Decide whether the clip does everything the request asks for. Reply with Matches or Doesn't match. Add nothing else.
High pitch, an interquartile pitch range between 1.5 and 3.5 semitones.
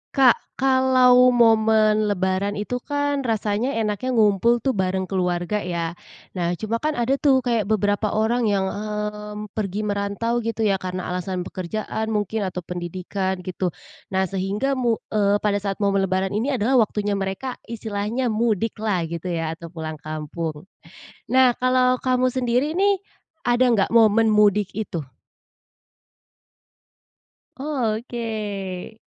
Doesn't match